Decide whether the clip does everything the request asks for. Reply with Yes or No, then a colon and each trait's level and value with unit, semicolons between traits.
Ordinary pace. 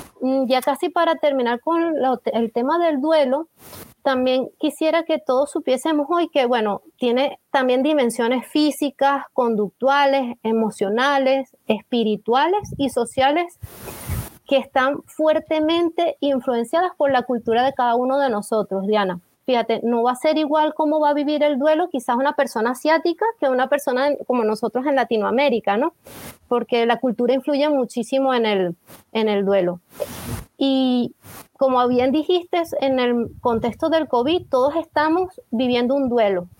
Yes: average, 145 wpm